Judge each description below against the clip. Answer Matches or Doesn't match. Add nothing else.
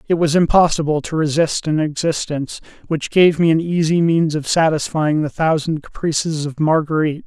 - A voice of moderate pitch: Matches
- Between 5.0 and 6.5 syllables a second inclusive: Matches